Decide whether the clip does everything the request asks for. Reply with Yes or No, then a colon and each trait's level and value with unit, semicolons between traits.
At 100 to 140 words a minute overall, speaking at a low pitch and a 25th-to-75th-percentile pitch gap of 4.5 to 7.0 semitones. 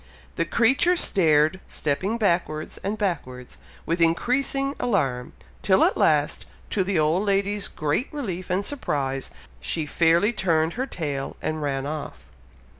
No: slow, 135 wpm; medium, 170 Hz; wide, 5.5 semitones